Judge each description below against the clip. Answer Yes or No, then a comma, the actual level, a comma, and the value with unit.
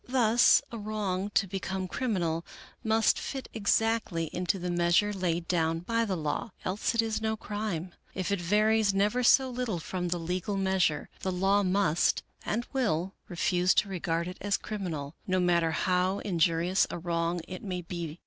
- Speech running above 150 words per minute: Yes, average, 170 wpm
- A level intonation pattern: No, average, 3.4 semitones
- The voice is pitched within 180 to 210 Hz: Yes, medium, 185 Hz